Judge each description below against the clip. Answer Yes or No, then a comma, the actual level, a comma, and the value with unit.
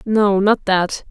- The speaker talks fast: No, average, 160 wpm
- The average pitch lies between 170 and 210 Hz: Yes, high, 200 Hz